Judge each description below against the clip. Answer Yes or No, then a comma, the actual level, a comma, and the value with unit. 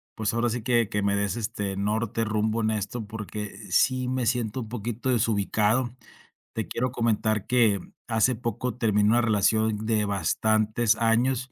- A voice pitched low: Yes, low, 110 Hz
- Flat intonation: Yes, narrow, 2.2 semitones